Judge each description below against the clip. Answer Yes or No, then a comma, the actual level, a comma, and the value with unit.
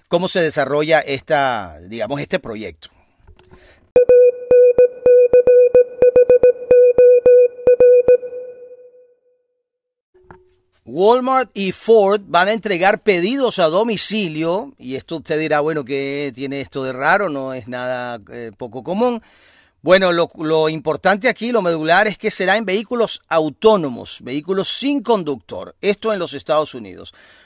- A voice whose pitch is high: Yes, high, 205 Hz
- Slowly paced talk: Yes, slow, 115 wpm